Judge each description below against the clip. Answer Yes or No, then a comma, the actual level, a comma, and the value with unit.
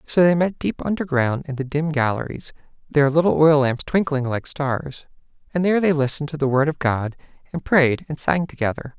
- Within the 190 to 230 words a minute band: Yes, average, 200 wpm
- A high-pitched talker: No, medium, 145 Hz